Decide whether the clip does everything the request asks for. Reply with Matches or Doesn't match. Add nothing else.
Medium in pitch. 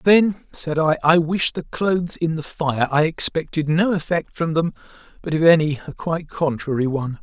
Matches